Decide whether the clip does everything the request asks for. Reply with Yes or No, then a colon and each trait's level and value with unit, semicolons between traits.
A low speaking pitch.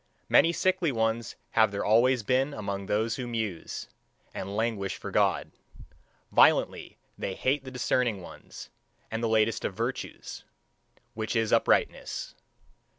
Yes: low, 115 Hz